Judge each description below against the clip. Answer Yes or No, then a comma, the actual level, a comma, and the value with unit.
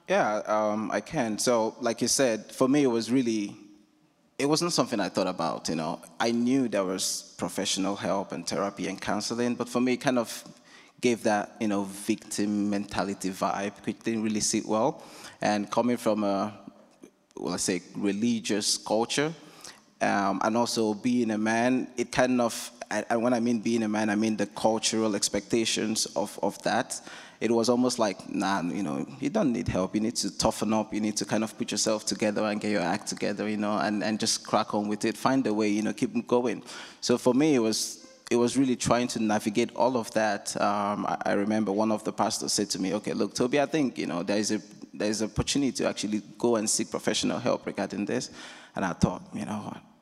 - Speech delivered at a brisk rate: Yes, fast, 215 wpm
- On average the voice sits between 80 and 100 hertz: No, low, 110 Hz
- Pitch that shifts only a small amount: Yes, narrow, 2.2 semitones